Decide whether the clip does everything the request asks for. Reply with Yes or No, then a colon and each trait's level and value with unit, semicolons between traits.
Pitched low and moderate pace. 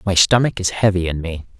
No: very low, 95 Hz; fast, 225 wpm